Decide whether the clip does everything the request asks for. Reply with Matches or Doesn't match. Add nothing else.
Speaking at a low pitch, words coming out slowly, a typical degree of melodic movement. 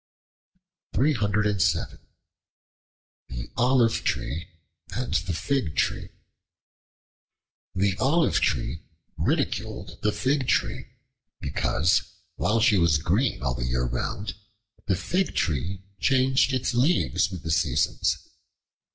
Doesn't match